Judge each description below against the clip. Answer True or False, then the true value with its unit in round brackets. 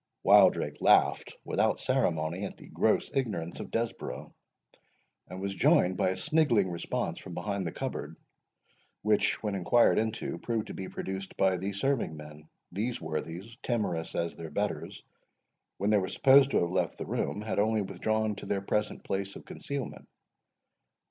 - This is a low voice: True (100 Hz)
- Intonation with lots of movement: False (3.9 semitones)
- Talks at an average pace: True (160 wpm)